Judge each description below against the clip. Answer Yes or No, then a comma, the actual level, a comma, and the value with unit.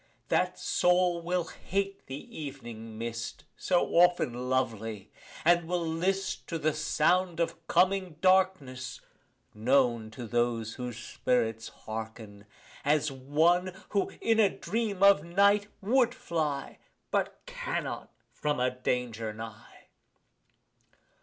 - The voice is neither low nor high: Yes, medium, 150 Hz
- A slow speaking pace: Yes, slow, 120 wpm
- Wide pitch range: Yes, wide, 7.4 semitones